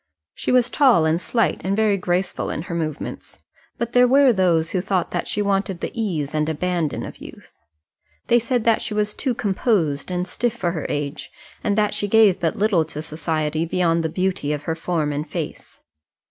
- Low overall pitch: No, medium, 180 Hz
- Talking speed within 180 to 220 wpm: Yes, average, 200 wpm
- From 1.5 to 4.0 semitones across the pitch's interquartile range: No, average, 4.9 semitones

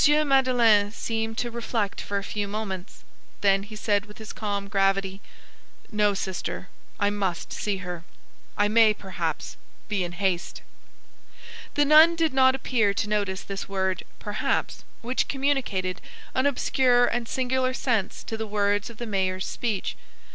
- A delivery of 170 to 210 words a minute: No, average, 150 wpm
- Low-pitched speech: No, high, 210 Hz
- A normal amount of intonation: Yes, average, 3.6 semitones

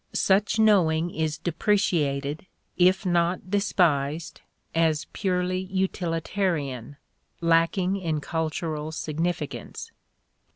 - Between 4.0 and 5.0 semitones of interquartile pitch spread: No, average, 3.1 semitones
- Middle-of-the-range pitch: Yes, medium, 170 Hz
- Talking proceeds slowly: Yes, slow, 80 wpm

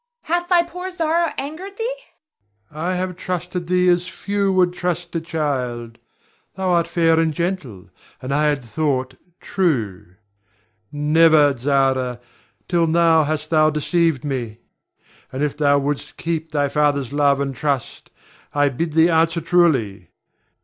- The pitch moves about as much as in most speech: Yes, average, 4.0 semitones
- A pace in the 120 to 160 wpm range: Yes, average, 145 wpm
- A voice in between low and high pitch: Yes, medium, 160 Hz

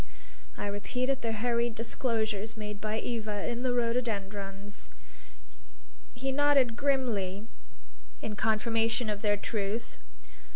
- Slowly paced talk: Yes, slow, 110 wpm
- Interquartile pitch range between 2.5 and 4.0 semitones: Yes, average, 2.8 semitones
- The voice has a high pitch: Yes, high, 225 Hz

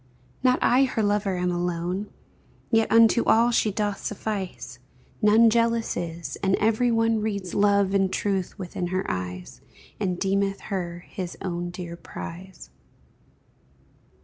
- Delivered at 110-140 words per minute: Yes, slow, 135 wpm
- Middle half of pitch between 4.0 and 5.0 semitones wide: No, average, 3.6 semitones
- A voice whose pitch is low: No, high, 195 Hz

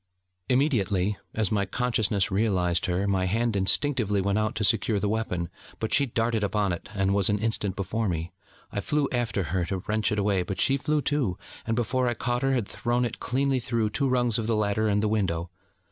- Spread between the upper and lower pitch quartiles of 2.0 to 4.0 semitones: Yes, average, 3.5 semitones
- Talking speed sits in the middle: No, fast, 210 wpm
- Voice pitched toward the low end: Yes, low, 105 Hz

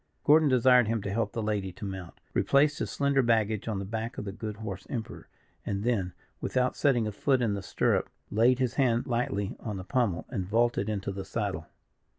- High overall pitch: No, low, 110 Hz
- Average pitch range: Yes, average, 3.8 semitones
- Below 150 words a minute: No, fast, 205 wpm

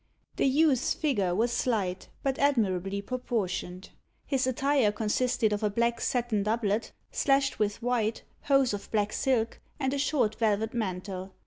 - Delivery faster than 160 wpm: No, average, 145 wpm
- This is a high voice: Yes, high, 225 Hz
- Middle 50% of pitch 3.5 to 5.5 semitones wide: Yes, average, 4.1 semitones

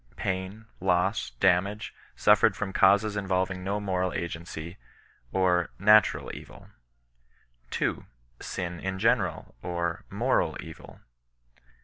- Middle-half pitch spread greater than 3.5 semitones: No, narrow, 2.4 semitones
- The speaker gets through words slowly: Yes, slow, 100 wpm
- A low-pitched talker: Yes, very low, 95 Hz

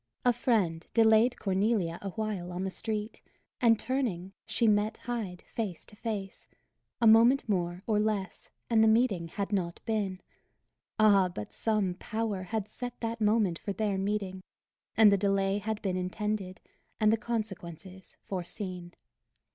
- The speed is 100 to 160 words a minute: Yes, average, 150 wpm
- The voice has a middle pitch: No, high, 205 Hz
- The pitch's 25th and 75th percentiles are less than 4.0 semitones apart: Yes, average, 3.0 semitones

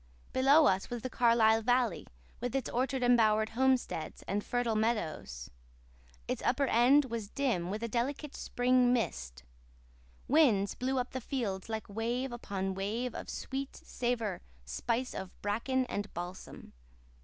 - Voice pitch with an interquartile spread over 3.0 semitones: Yes, average, 3.9 semitones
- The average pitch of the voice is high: Yes, high, 235 Hz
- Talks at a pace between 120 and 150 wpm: Yes, average, 145 wpm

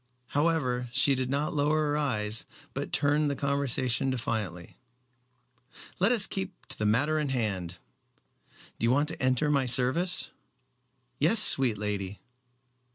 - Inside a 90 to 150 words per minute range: Yes, average, 140 wpm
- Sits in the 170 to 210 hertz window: No, low, 135 Hz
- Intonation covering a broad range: No, average, 4.4 semitones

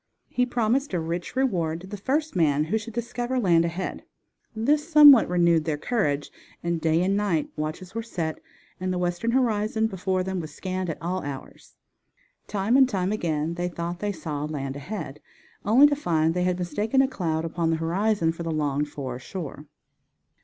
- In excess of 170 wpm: Yes, average, 180 wpm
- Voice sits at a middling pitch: Yes, medium, 180 Hz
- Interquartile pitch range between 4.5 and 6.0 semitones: Yes, average, 5.3 semitones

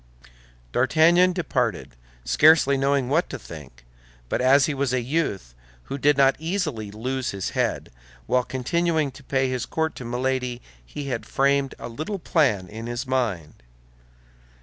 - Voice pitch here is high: No, low, 135 Hz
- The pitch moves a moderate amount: Yes, average, 3.7 semitones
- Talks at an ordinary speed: Yes, average, 150 wpm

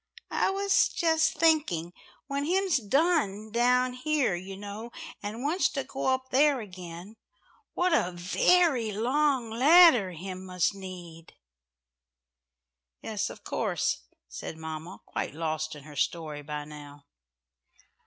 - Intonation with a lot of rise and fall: Yes, wide, 8.9 semitones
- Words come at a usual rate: No, slow, 125 wpm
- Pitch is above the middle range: Yes, high, 215 Hz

